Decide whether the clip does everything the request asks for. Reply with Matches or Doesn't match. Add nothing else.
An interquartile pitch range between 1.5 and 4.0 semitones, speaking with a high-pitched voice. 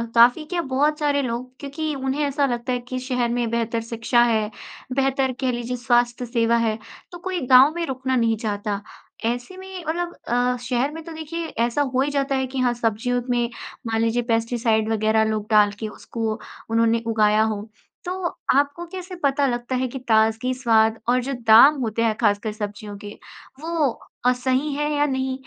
Matches